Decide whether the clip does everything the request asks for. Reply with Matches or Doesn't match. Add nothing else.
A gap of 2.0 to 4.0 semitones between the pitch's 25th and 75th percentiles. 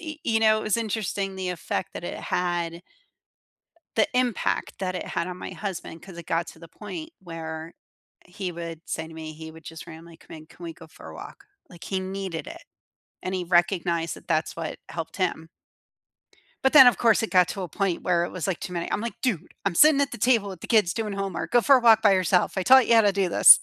Doesn't match